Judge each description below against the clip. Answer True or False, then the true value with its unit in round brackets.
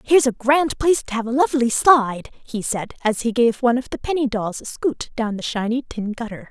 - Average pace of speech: False (240 wpm)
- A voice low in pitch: False (245 Hz)